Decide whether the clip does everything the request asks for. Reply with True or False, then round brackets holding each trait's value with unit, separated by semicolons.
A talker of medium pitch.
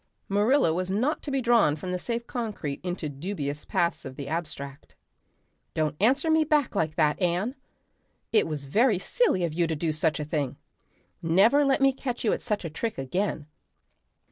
True (180 Hz)